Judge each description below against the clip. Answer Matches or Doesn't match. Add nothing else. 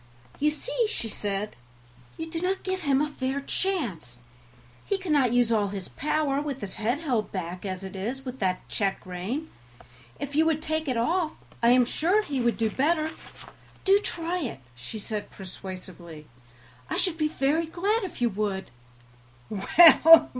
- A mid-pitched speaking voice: Doesn't match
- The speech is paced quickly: Doesn't match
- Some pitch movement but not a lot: Doesn't match